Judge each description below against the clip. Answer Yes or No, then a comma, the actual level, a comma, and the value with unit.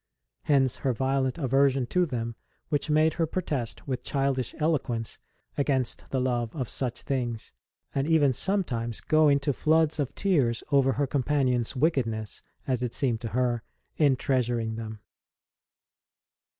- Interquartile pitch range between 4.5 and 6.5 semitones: No, average, 3.4 semitones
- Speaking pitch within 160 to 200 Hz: No, low, 130 Hz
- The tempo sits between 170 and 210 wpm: No, average, 140 wpm